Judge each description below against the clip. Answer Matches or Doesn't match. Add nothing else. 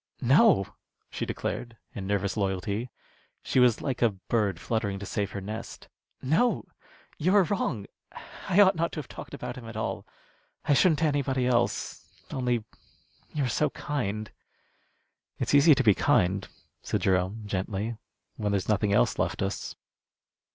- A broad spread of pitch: Matches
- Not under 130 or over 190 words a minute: Matches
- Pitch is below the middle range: Matches